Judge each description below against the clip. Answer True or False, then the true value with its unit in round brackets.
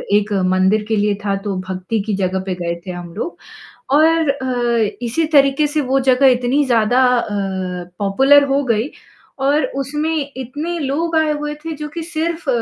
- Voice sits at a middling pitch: False (265 Hz)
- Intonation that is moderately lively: False (6.2 semitones)